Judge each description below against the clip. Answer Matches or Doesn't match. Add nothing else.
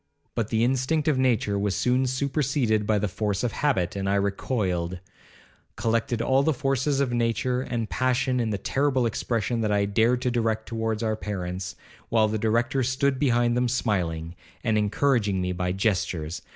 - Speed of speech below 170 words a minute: Doesn't match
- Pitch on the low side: Matches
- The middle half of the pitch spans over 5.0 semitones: Doesn't match